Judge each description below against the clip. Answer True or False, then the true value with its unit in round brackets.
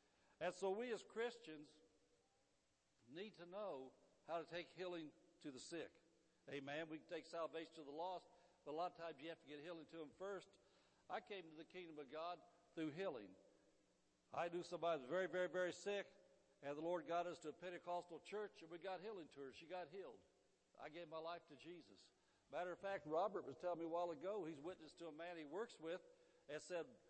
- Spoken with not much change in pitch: True (2.2 semitones)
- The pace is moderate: False (220 wpm)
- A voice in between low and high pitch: True (170 Hz)